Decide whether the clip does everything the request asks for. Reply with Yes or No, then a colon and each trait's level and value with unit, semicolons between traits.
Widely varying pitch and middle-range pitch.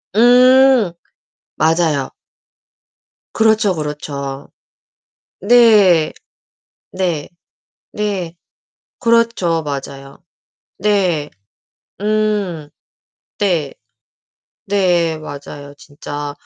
Yes: wide, 6.2 semitones; medium, 175 Hz